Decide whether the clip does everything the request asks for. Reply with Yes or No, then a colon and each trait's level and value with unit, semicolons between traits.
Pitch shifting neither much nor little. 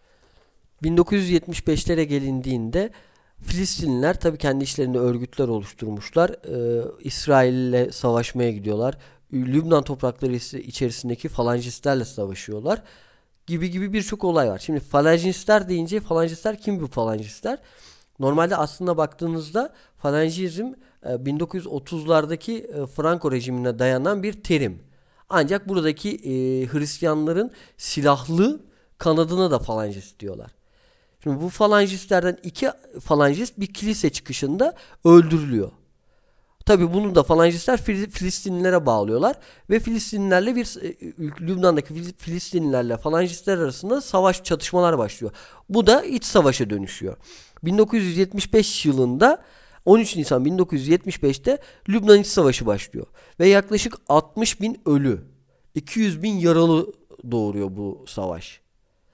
No: wide, 6.8 semitones